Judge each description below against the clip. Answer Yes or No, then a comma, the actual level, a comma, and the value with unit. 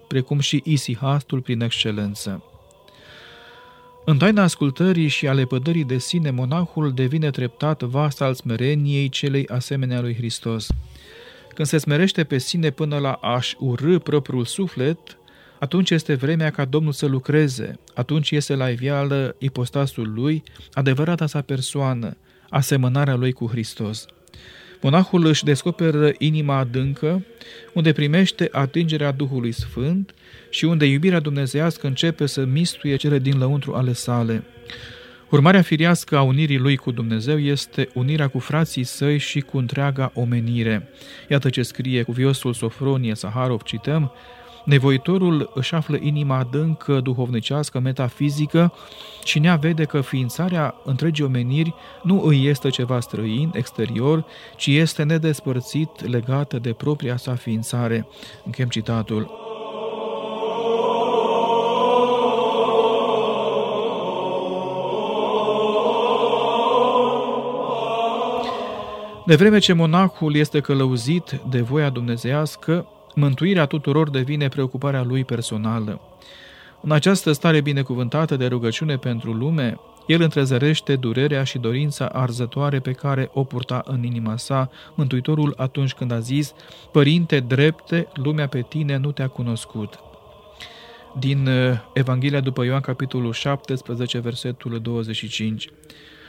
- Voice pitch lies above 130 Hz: Yes, medium, 140 Hz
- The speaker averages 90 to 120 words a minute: Yes, slow, 115 wpm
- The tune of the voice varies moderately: Yes, average, 3.8 semitones